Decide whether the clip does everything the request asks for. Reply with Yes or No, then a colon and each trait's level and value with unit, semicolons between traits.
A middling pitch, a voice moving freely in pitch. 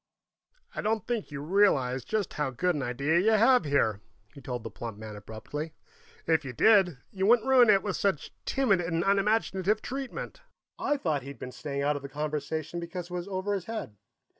Yes: medium, 170 Hz; wide, 6.6 semitones